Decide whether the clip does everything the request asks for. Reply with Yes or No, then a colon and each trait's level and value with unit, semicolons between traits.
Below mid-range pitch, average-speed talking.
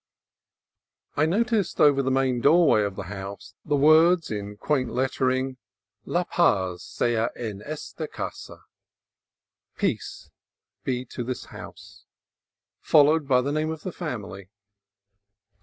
No: low, 130 Hz; slow, 125 wpm